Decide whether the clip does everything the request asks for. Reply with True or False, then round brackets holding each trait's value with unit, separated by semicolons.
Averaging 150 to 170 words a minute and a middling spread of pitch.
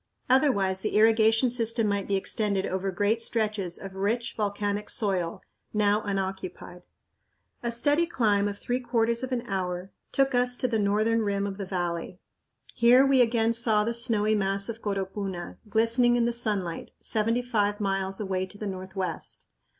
True (165 wpm; 3.2 semitones)